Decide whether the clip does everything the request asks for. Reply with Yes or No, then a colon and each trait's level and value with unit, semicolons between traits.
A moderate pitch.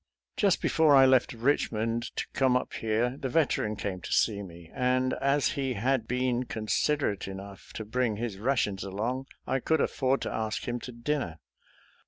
No: low, 120 Hz